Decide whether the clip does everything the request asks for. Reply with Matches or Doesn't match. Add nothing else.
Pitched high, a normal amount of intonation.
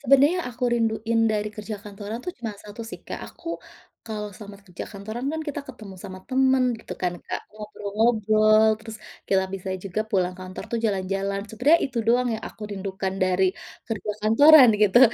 Matches